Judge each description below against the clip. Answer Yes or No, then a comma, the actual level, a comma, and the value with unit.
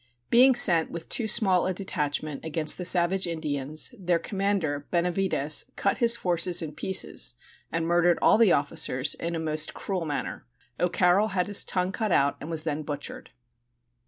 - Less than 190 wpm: Yes, average, 165 wpm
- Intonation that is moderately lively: Yes, average, 3.6 semitones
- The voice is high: No, medium, 170 Hz